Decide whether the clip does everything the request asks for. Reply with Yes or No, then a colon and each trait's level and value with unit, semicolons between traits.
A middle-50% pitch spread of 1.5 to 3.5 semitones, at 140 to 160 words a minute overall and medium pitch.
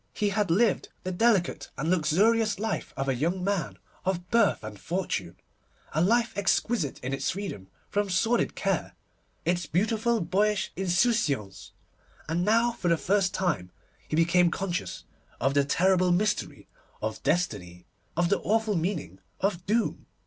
No: average, 4.6 semitones; average, 150 wpm; medium, 180 Hz